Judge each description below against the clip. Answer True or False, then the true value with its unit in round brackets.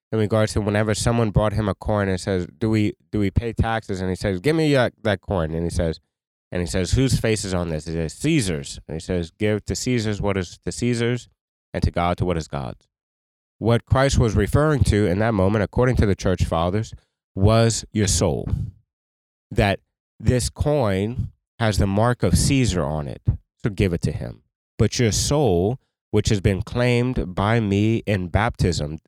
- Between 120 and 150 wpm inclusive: False (200 wpm)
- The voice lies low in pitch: True (105 Hz)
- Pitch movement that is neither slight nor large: True (4.0 semitones)